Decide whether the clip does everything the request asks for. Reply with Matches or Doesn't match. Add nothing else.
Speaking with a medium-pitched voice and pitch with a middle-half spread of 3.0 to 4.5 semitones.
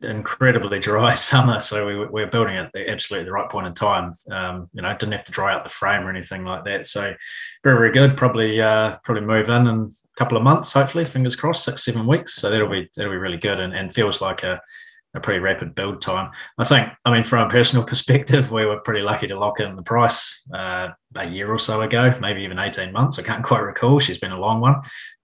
Doesn't match